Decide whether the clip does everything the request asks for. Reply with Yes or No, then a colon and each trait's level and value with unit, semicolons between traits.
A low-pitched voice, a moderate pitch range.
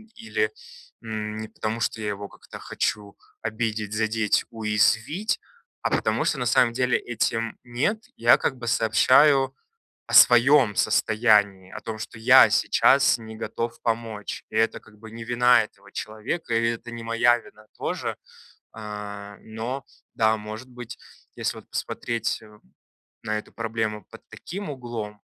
No: low, 115 Hz; narrow, 2.0 semitones